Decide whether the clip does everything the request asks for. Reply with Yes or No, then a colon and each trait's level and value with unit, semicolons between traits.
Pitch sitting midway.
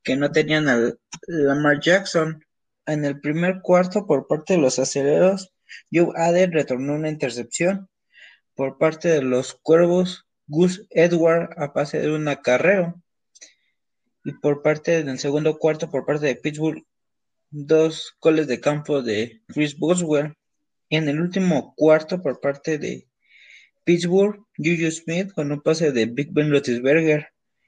Yes: medium, 155 Hz